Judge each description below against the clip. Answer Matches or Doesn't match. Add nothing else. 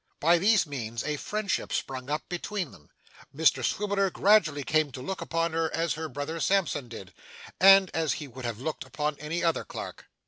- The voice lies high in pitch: Doesn't match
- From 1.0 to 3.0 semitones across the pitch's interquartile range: Doesn't match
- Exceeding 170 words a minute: Matches